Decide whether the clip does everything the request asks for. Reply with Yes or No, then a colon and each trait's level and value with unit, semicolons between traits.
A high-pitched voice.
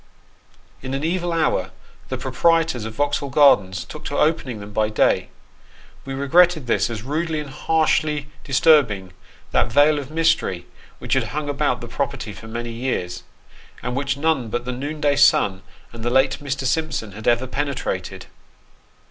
No: medium, 140 Hz